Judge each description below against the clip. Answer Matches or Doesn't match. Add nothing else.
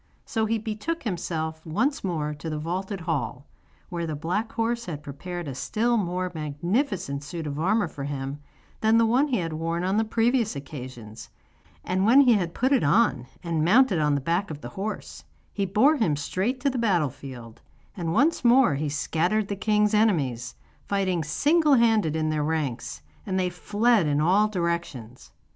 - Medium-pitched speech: Matches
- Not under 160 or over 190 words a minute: Matches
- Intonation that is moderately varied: Doesn't match